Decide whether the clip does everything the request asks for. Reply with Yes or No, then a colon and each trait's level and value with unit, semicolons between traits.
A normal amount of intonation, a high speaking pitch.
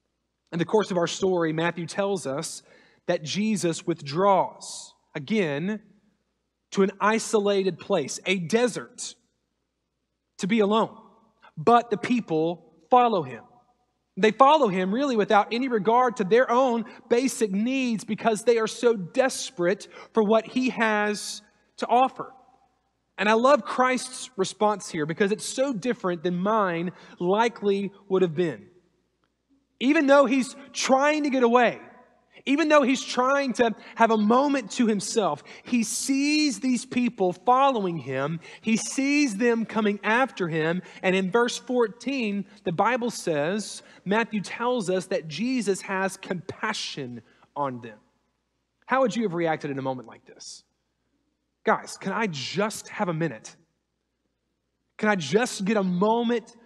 Yes: average, 4.5 semitones; high, 215 Hz